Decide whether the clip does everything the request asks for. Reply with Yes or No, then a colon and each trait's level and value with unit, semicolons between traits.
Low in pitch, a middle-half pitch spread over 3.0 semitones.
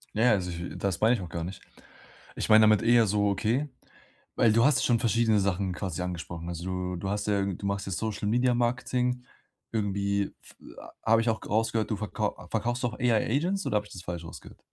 Yes: low, 105 Hz; average, 3.4 semitones